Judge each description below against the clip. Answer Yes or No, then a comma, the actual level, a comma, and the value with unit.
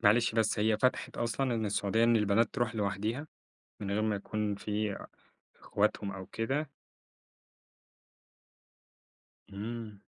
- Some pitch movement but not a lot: No, narrow, 2.2 semitones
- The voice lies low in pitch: Yes, low, 110 Hz